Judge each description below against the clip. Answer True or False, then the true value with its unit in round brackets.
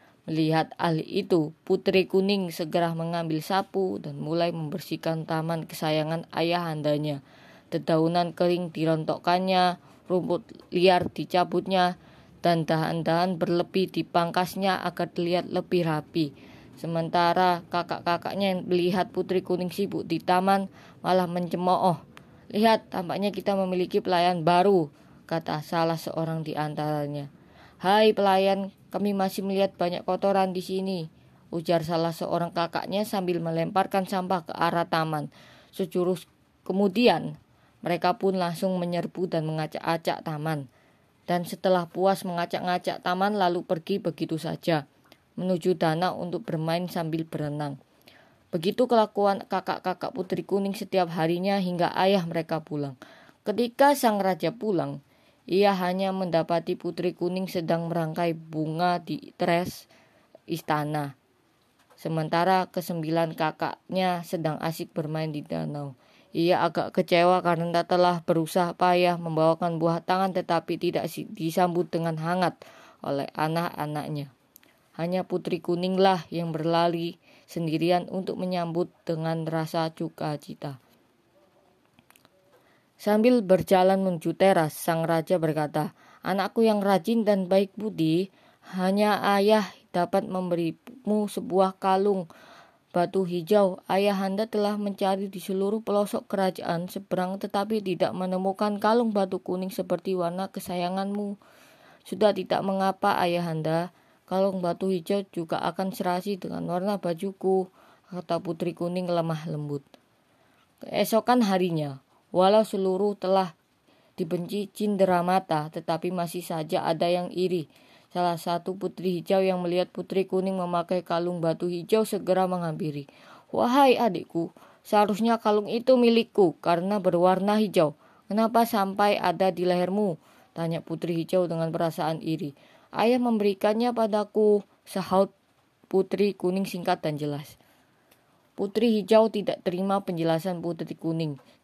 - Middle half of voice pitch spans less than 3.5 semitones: True (2.5 semitones)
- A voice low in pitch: False (180 Hz)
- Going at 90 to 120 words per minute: True (115 wpm)